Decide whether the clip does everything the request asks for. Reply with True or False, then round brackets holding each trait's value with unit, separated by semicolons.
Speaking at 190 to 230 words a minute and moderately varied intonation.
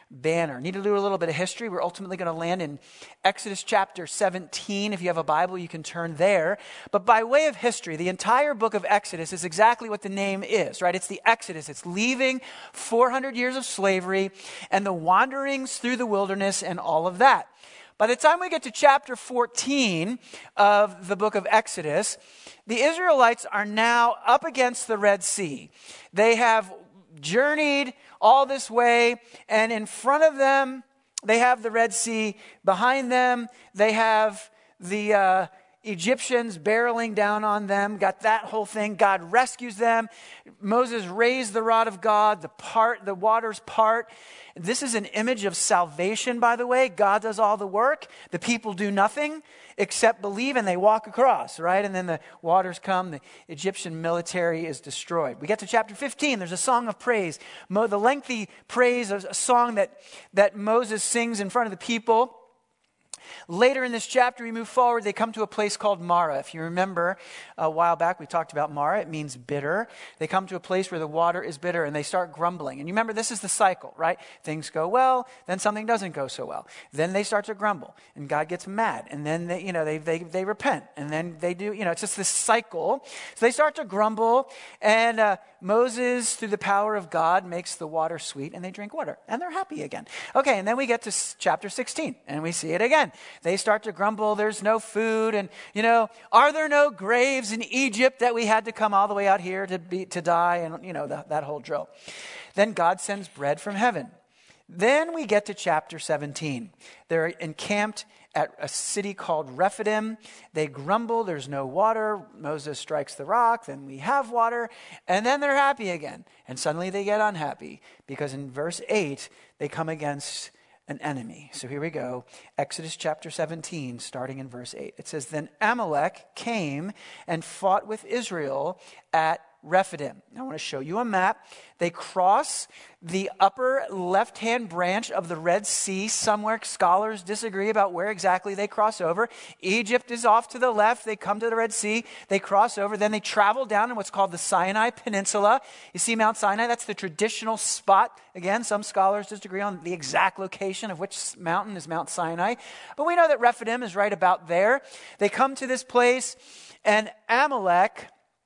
True (195 wpm; 4.7 semitones)